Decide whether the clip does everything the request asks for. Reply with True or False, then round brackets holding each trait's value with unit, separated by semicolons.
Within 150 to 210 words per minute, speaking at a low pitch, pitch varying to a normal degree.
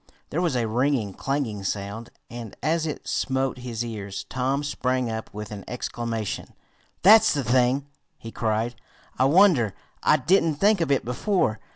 True (160 wpm; 125 Hz; 4.5 semitones)